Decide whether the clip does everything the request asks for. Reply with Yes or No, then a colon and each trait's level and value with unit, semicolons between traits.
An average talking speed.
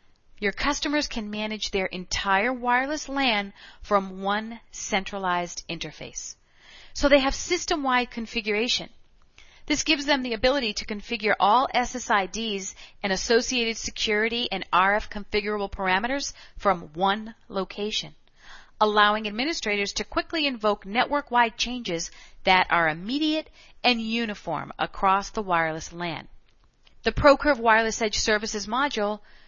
No: slow, 120 wpm